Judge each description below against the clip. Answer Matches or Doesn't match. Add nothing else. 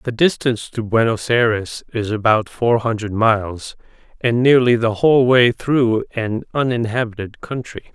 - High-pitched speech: Doesn't match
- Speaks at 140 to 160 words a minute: Matches